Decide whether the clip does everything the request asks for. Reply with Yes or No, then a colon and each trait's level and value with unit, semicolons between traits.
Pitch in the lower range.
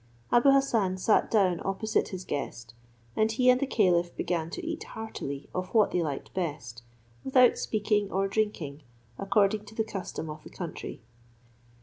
No: high, 195 Hz